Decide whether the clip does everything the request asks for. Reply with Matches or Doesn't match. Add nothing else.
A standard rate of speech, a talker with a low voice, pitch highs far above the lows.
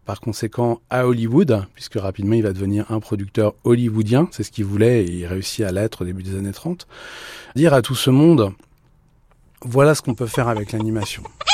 Doesn't match